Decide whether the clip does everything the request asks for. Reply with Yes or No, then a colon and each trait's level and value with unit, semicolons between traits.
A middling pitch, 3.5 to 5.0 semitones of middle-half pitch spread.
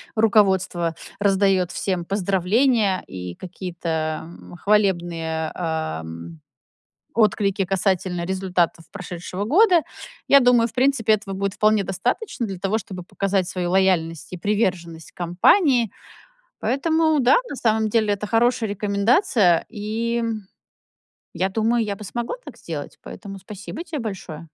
No: high, 195 Hz; average, 4.1 semitones